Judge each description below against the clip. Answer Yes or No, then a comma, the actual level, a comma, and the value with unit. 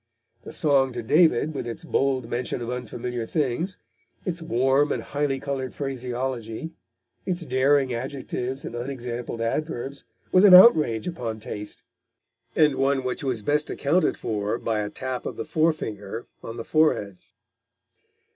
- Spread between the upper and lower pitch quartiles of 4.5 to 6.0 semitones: No, average, 3.8 semitones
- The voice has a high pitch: No, low, 130 Hz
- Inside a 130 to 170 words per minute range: Yes, average, 145 wpm